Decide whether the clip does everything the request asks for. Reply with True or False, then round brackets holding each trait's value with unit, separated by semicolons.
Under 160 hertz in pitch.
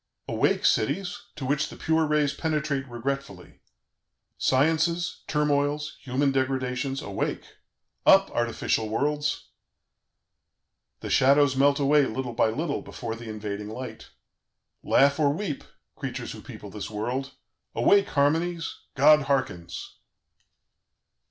True (140 Hz)